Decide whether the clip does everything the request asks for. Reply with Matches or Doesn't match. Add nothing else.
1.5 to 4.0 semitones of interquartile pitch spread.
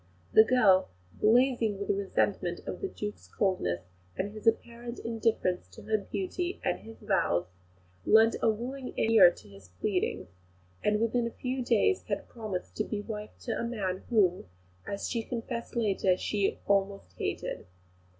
Matches